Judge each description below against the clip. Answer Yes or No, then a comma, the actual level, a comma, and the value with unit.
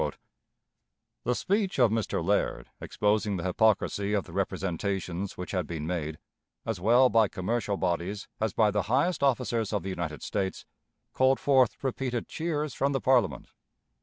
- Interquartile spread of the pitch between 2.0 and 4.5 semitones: No, average, 5.3 semitones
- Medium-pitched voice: No, low, 105 Hz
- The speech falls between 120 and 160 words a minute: Yes, average, 155 wpm